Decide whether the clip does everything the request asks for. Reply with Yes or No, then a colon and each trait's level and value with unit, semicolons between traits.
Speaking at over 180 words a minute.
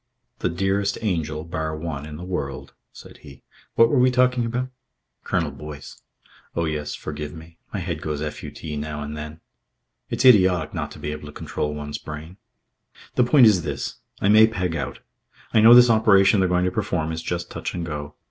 Yes: average, 195 wpm